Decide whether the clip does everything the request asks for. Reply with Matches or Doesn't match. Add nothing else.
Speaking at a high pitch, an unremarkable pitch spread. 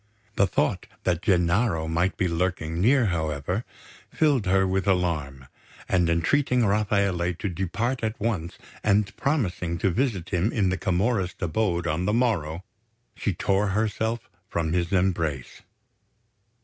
Doesn't match